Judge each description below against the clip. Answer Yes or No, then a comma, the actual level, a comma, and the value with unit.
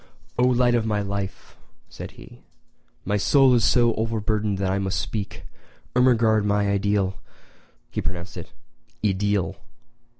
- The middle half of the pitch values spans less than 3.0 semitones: Yes, narrow, 2.6 semitones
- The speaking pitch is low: Yes, low, 105 Hz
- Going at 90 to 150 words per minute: Yes, average, 140 wpm